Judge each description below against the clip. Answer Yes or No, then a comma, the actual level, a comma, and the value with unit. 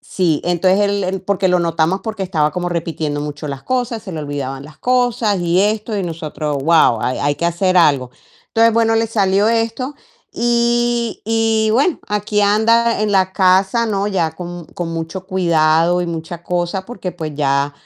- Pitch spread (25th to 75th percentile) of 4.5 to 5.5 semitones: Yes, average, 5.1 semitones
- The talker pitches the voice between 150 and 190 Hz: Yes, medium, 185 Hz